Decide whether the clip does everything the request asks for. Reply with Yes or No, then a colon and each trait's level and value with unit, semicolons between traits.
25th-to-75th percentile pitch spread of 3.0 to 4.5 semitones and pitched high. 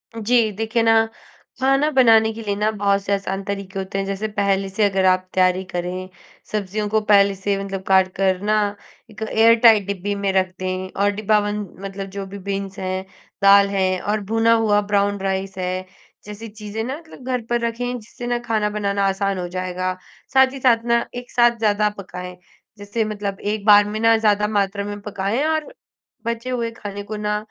No: narrow, 2.4 semitones; high, 205 Hz